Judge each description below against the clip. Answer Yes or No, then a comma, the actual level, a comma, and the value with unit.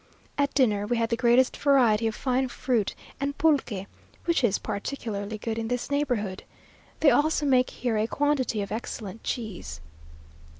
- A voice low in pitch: No, high, 240 Hz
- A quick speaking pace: No, average, 160 wpm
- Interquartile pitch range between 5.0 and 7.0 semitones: No, average, 4.2 semitones